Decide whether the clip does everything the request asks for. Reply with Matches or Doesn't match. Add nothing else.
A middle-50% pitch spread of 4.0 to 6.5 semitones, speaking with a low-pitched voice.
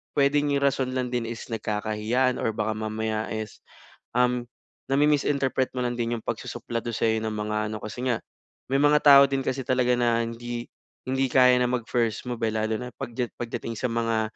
Doesn't match